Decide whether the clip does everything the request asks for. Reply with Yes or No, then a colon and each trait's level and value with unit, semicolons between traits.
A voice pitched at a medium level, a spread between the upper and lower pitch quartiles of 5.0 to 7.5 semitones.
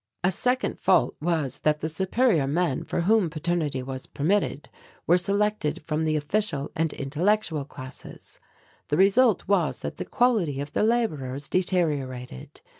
Yes: medium, 165 Hz; wide, 5.4 semitones